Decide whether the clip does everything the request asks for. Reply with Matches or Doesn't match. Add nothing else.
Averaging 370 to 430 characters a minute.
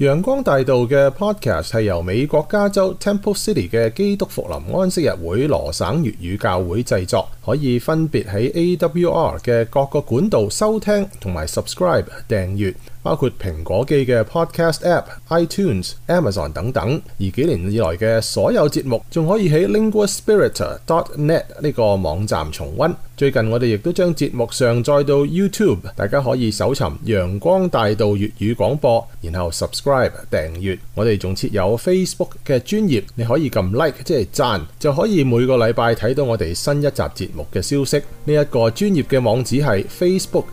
Matches